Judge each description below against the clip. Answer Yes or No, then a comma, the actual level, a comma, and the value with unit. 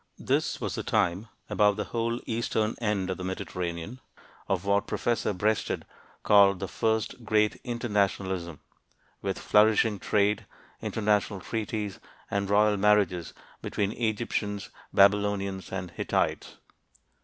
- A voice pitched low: Yes, low, 105 Hz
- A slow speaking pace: Yes, slow, 120 wpm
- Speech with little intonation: Yes, narrow, 1.9 semitones